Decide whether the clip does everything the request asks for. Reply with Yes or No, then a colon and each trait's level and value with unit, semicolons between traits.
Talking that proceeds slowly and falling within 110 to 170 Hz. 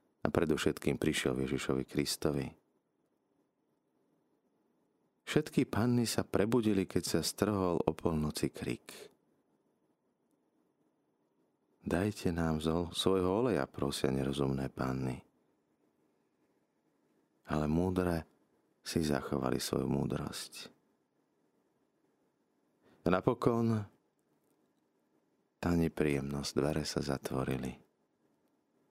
No: slow, 75 wpm; very low, 80 Hz